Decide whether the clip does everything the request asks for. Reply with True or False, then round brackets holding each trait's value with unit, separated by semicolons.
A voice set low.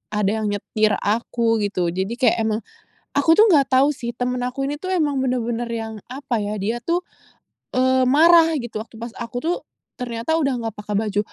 False (240 Hz)